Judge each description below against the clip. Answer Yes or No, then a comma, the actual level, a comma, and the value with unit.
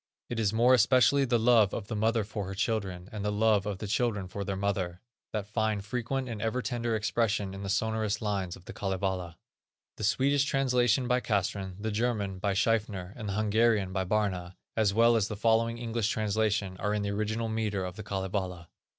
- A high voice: No, low, 105 Hz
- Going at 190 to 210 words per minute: Yes, average, 200 wpm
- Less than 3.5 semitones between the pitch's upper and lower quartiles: Yes, narrow, 2.6 semitones